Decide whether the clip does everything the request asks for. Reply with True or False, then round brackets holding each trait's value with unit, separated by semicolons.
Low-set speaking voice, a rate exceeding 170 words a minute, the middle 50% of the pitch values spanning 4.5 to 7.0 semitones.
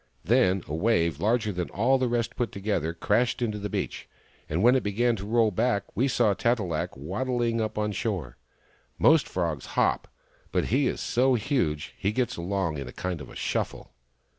True (105 Hz; 195 wpm; 5.3 semitones)